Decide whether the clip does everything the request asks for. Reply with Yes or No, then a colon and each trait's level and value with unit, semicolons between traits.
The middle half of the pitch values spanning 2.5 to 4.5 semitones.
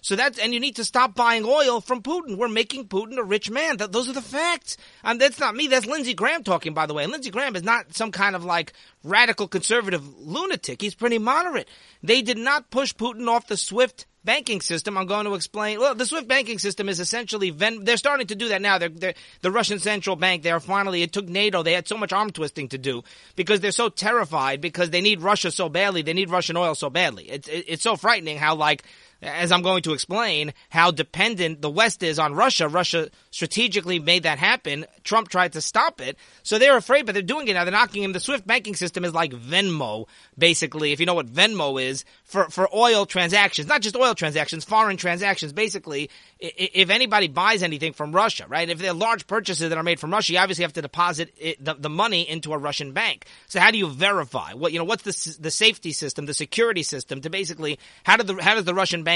No: average, 5.3 semitones